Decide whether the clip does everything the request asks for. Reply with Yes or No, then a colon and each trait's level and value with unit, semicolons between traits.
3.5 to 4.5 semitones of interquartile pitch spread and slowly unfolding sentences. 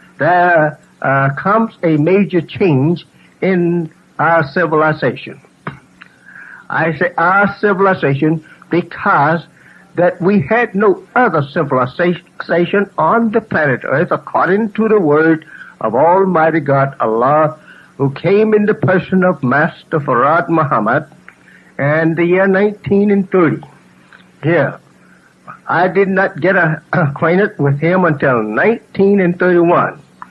Yes: average, 3.8 semitones; slow, 110 wpm